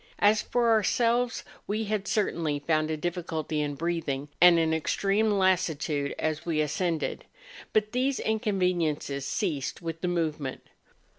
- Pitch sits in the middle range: Yes, medium, 170 Hz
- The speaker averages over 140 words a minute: No, slow, 135 wpm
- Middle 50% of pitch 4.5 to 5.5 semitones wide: Yes, average, 5.1 semitones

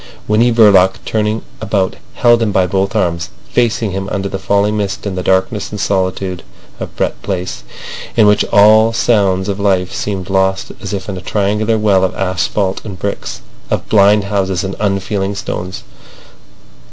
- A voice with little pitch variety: Yes, narrow, 1.9 semitones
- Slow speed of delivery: No, average, 165 wpm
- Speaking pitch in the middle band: No, low, 100 Hz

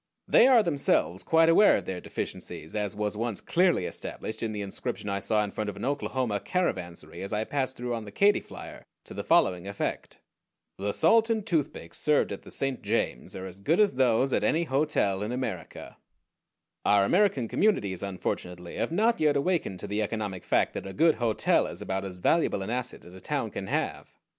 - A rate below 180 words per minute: No, average, 200 wpm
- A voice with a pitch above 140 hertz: No, low, 110 Hz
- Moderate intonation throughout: No, wide, 7.9 semitones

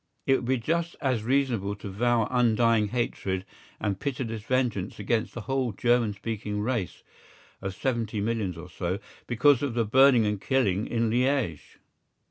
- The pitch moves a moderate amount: Yes, average, 3.7 semitones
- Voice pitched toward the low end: Yes, low, 115 Hz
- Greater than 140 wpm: Yes, average, 155 wpm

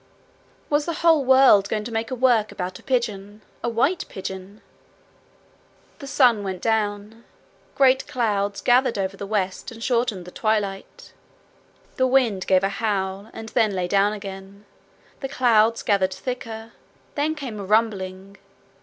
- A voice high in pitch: Yes, high, 215 Hz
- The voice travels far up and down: No, average, 3.9 semitones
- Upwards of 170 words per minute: No, average, 150 wpm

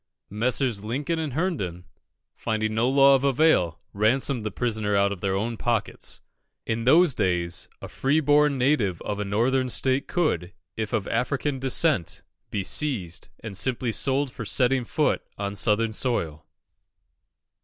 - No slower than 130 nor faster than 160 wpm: Yes, average, 150 wpm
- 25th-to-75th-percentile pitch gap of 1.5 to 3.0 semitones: No, average, 5.0 semitones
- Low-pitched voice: Yes, low, 115 Hz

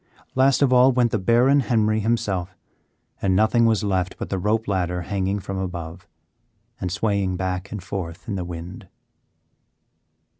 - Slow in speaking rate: No, average, 155 wpm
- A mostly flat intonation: No, average, 3.5 semitones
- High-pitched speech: No, low, 100 Hz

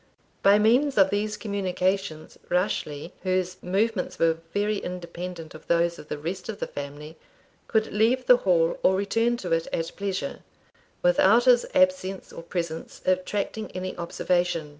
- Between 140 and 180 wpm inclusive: Yes, average, 150 wpm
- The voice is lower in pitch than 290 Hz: Yes, medium, 185 Hz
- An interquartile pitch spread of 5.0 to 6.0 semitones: No, average, 3.8 semitones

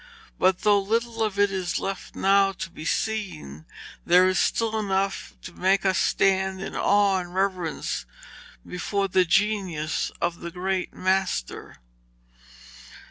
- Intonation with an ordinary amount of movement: No, narrow, 1.9 semitones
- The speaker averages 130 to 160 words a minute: Yes, slow, 135 wpm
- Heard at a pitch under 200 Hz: Yes, high, 190 Hz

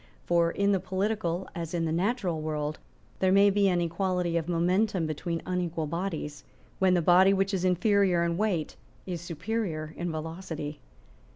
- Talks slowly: No, average, 165 wpm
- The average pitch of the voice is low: No, medium, 175 Hz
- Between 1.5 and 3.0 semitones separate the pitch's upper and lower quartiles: Yes, narrow, 2.6 semitones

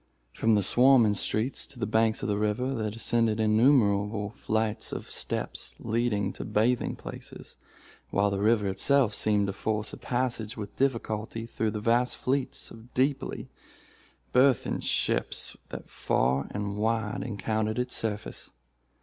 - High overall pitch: No, low, 110 Hz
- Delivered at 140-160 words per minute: Yes, average, 145 wpm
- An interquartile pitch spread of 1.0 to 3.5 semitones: Yes, average, 2.7 semitones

